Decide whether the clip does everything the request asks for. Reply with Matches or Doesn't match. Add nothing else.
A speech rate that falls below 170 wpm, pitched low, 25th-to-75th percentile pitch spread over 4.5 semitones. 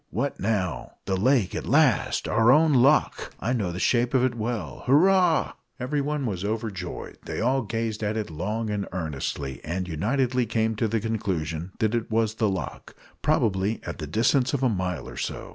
Doesn't match